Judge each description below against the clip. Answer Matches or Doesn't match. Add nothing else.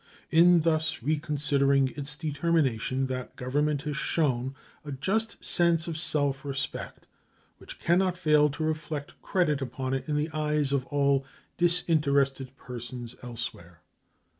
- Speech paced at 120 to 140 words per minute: Matches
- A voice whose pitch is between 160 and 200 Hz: Doesn't match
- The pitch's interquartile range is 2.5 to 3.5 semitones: Matches